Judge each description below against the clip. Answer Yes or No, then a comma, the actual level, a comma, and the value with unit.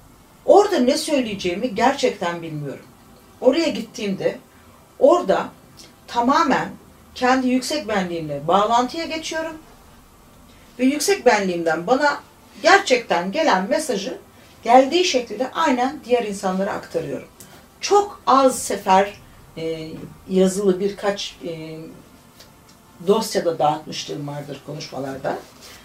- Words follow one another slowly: Yes, slow, 85 wpm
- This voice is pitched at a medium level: No, high, 210 Hz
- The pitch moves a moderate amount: No, wide, 8.0 semitones